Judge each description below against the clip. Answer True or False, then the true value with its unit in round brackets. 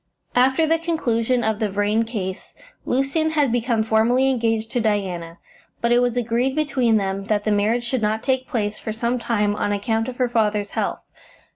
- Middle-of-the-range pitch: False (230 Hz)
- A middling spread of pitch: True (3.1 semitones)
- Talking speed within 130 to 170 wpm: False (185 wpm)